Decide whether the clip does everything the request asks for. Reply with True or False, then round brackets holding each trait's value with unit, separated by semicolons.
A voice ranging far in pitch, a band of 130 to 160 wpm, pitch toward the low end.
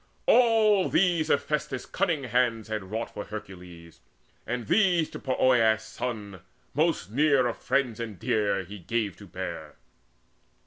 True (6.2 semitones; 135 wpm; 120 Hz)